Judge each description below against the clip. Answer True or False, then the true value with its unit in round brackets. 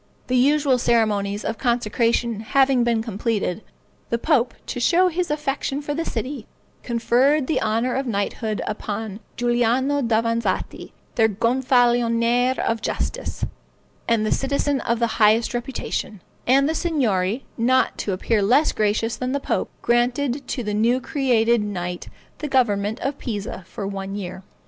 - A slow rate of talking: False (145 wpm)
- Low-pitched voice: False (235 Hz)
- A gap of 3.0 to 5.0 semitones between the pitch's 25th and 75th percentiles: True (3.4 semitones)